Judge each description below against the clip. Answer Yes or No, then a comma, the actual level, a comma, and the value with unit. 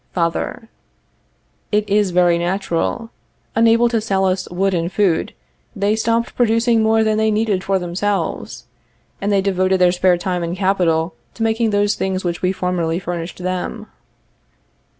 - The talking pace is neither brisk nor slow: Yes, average, 150 wpm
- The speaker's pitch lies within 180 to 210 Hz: Yes, high, 190 Hz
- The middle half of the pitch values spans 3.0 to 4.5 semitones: Yes, average, 3.4 semitones